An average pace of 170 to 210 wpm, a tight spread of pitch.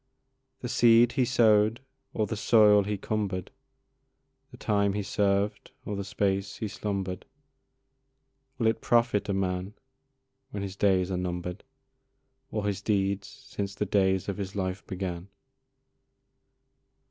No: slow, 135 wpm; narrow, 1.8 semitones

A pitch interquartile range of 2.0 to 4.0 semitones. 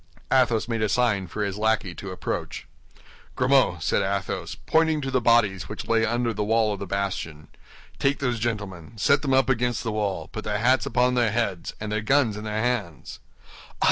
Yes: average, 3.7 semitones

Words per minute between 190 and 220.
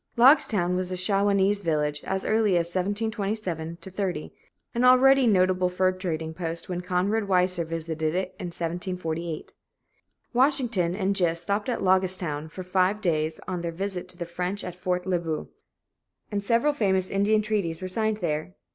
No: average, 165 wpm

